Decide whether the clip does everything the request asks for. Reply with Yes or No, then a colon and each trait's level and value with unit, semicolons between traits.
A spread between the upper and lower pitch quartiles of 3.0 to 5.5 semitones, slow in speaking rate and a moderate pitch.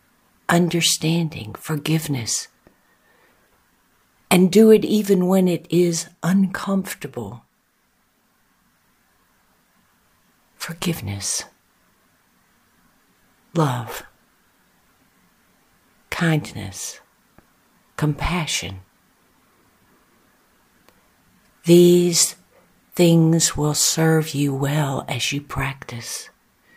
Yes: average, 3.9 semitones; slow, 50 wpm; medium, 160 Hz